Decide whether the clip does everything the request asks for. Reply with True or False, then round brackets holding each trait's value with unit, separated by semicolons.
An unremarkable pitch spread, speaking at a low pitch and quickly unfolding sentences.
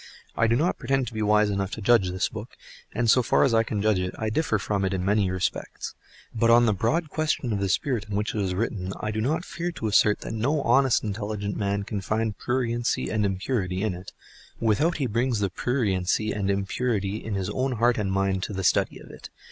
True (3.3 semitones; 110 Hz; 235 wpm)